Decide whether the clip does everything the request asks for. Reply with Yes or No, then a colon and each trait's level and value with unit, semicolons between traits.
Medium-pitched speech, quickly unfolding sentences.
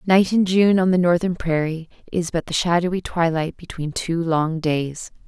No: medium, 170 Hz; average, 180 wpm